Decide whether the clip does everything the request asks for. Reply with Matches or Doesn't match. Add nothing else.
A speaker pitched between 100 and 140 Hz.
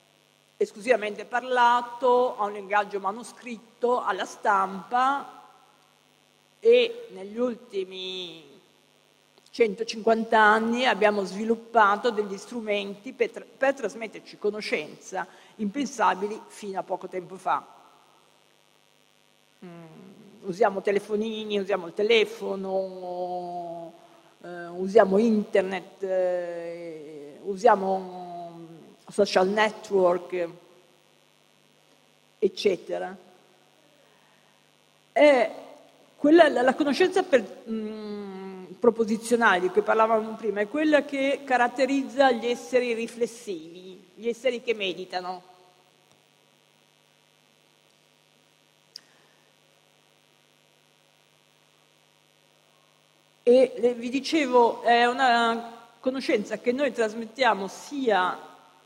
Doesn't match